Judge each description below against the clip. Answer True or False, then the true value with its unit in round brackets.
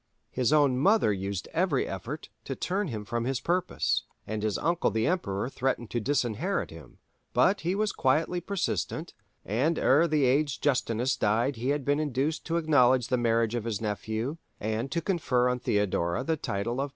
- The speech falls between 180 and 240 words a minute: True (185 wpm)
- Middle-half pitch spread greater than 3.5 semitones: True (5.5 semitones)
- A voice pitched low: True (130 Hz)